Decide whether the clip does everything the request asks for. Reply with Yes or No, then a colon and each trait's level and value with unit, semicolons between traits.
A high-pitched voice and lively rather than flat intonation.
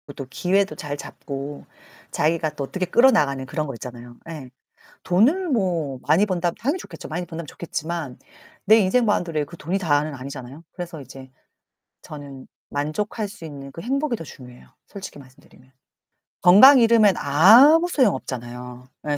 No: medium, 160 Hz; wide, 6.4 semitones